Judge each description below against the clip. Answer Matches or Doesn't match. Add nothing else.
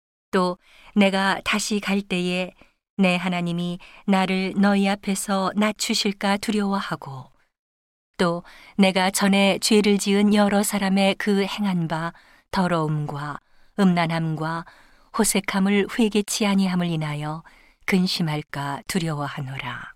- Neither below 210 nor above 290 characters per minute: Matches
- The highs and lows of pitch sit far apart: Doesn't match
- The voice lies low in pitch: Doesn't match